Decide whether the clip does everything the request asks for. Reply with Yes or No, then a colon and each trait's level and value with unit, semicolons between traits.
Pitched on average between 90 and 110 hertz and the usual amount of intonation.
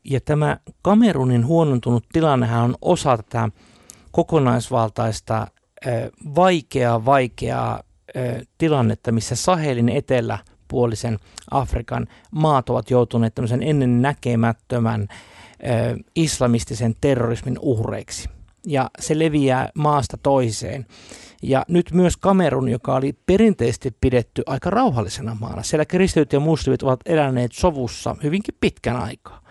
No: low, 125 Hz; average, 4.3 semitones